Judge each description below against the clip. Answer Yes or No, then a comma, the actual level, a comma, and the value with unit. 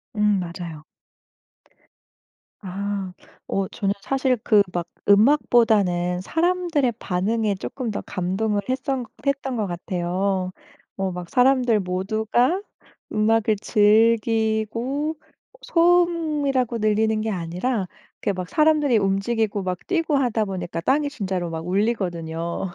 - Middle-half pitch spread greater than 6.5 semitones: No, average, 5.3 semitones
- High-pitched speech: Yes, high, 215 Hz